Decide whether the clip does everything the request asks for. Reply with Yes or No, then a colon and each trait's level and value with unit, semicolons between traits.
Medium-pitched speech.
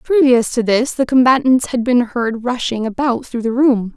No: high, 245 Hz